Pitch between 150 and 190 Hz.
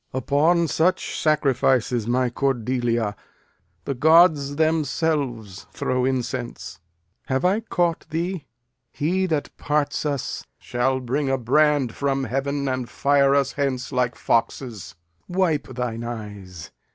No: low, 135 Hz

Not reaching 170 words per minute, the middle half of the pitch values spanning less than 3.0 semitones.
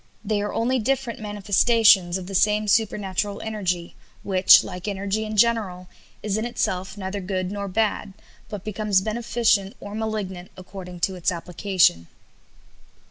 Yes: average, 140 wpm; narrow, 2.6 semitones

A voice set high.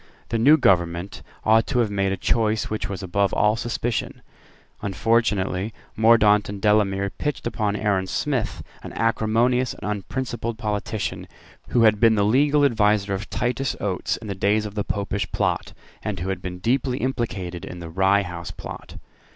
No: low, 105 Hz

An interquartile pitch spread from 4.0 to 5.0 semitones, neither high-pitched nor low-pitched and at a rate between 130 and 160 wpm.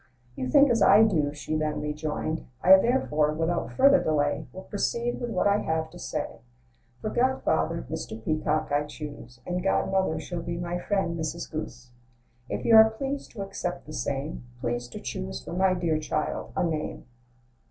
No: average, 4.7 semitones; medium, 160 Hz; average, 175 wpm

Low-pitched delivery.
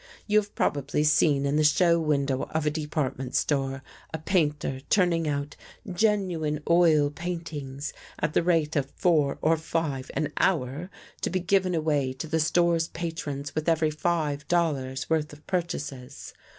No: medium, 155 Hz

